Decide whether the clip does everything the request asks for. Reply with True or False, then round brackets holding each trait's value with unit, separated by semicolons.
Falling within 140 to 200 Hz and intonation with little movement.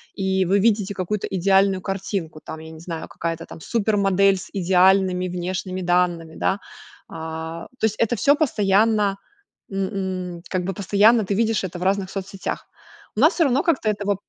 True (190 Hz; 2.2 semitones)